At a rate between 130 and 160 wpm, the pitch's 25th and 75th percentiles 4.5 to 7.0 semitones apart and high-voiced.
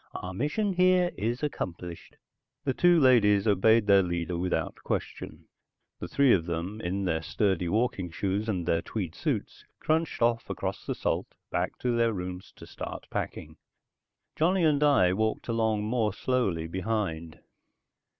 No: average, 150 wpm; wide, 5.6 semitones; low, 105 Hz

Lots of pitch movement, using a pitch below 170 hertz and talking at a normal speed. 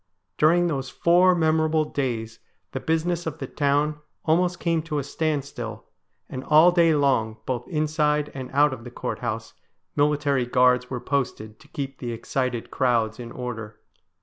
No: average, 4.2 semitones; medium, 140 Hz; average, 155 wpm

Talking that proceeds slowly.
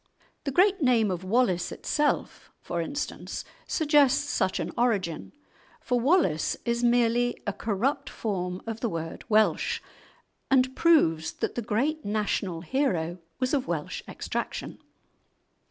Yes: slow, 130 wpm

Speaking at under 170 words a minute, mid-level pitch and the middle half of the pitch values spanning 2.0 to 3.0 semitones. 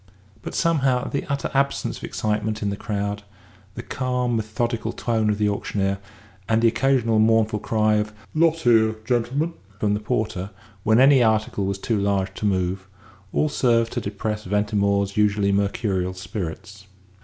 No: average, 155 wpm; low, 110 Hz; average, 2.7 semitones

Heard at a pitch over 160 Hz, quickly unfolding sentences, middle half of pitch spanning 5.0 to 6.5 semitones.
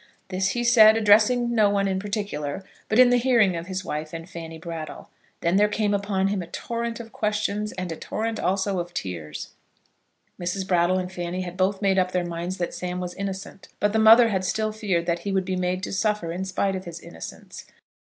No: high, 190 Hz; fast, 215 wpm; average, 3.1 semitones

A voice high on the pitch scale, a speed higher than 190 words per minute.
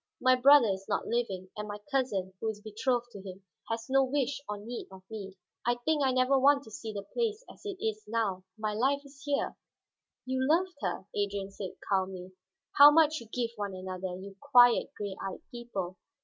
Yes: high, 225 Hz; average, 200 wpm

